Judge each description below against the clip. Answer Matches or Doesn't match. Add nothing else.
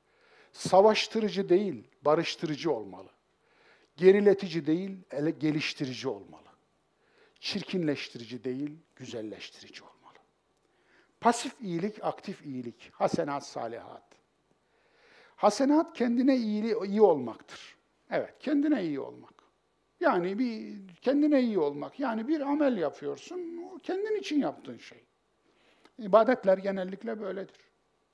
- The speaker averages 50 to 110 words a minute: Matches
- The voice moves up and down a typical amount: Doesn't match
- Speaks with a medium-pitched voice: Doesn't match